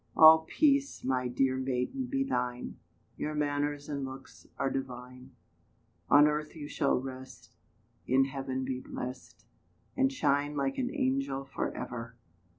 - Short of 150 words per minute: Yes, average, 140 wpm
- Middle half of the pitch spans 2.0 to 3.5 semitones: Yes, average, 2.8 semitones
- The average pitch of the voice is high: No, low, 135 Hz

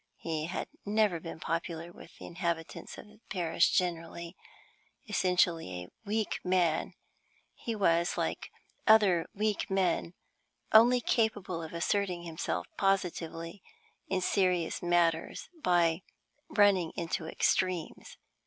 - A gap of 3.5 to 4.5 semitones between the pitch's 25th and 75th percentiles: No, average, 3.0 semitones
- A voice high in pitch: No, medium, 175 Hz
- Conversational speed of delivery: No, slow, 115 wpm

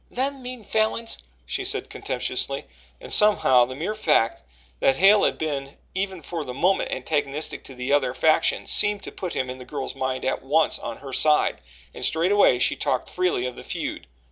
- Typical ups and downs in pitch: No, wide, 7.0 semitones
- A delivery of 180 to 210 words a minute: Yes, average, 190 wpm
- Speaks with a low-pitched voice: No, medium, 155 Hz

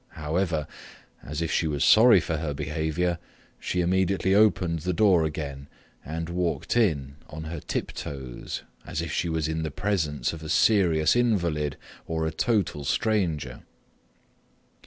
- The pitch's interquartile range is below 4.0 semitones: Yes, average, 3.2 semitones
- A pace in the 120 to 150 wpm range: Yes, average, 145 wpm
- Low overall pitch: Yes, very low, 80 Hz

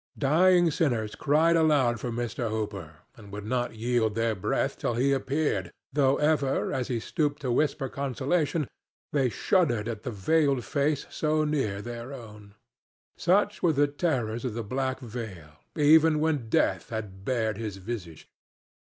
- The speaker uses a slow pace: No, average, 155 wpm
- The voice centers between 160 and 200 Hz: No, low, 125 Hz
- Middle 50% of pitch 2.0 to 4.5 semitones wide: No, average, 5.2 semitones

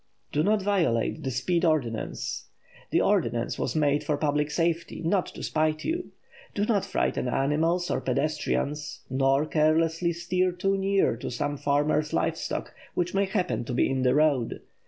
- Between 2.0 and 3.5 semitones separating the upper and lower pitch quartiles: No, average, 3.9 semitones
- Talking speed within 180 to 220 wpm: No, average, 165 wpm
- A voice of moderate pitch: Yes, medium, 155 Hz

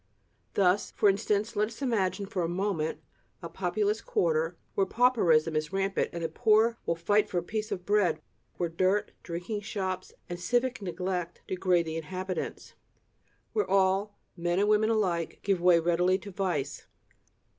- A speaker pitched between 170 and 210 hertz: Yes, high, 190 Hz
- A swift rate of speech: No, average, 160 wpm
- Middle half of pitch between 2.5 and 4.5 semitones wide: Yes, average, 3.3 semitones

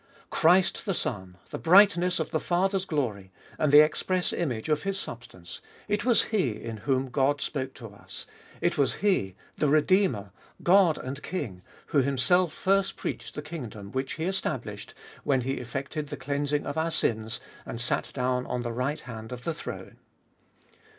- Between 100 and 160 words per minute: No, average, 170 wpm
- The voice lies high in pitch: No, medium, 140 Hz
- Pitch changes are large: Yes, wide, 6.0 semitones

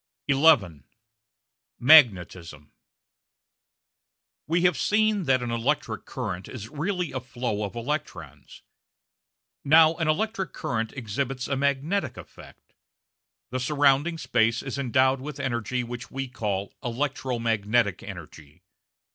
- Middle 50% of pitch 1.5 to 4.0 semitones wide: No, average, 4.8 semitones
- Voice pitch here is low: Yes, low, 130 Hz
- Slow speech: Yes, slow, 115 wpm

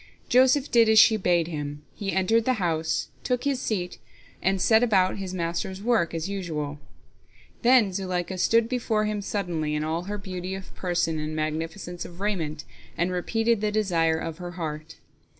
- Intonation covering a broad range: No, average, 4.5 semitones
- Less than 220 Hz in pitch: Yes, medium, 185 Hz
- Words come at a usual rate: Yes, average, 170 wpm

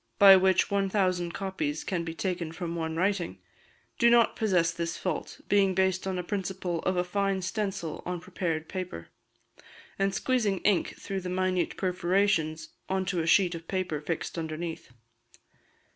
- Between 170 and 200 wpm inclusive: No, average, 160 wpm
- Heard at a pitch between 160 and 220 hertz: Yes, medium, 185 Hz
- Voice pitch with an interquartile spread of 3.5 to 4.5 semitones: No, narrow, 2.5 semitones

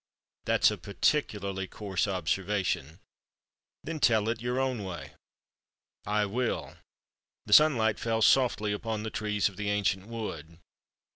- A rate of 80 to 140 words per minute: Yes, slow, 135 wpm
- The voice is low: Yes, low, 105 Hz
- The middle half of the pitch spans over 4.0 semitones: No, average, 2.9 semitones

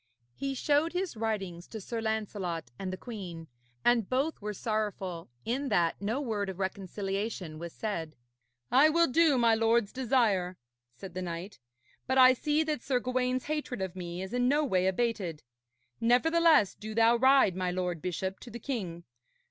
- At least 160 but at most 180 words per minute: Yes, average, 170 wpm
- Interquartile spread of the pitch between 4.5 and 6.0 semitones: Yes, wide, 5.6 semitones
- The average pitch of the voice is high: Yes, high, 220 Hz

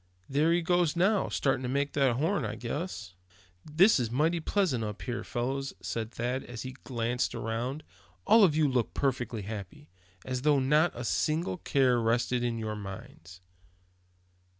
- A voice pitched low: Yes, low, 130 Hz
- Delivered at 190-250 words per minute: No, average, 165 wpm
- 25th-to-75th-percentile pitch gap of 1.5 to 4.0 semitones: No, average, 4.7 semitones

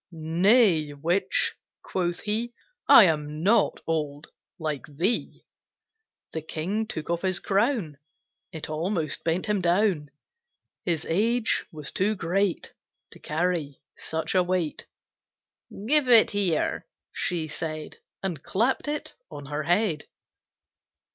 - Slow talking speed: Yes, slow, 120 wpm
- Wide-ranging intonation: No, average, 4.7 semitones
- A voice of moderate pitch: Yes, medium, 175 Hz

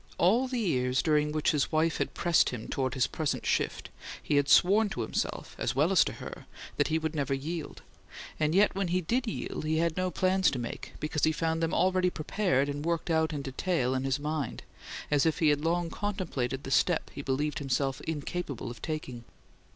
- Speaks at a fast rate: Yes, fast, 210 wpm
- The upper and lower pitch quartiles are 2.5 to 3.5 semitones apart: No, average, 3.9 semitones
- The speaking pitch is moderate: Yes, medium, 155 Hz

